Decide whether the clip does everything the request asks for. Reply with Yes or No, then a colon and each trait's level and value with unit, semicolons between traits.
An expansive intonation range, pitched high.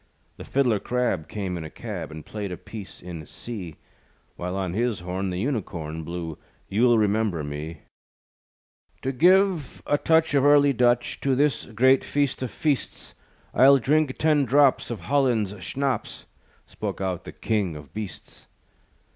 No: wide, 7.2 semitones; low, 115 Hz